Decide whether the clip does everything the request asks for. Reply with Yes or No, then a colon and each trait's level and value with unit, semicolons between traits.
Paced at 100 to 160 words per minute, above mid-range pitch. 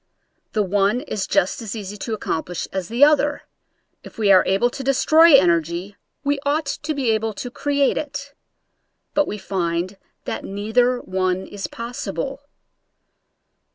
Yes: average, 155 wpm; high, 220 Hz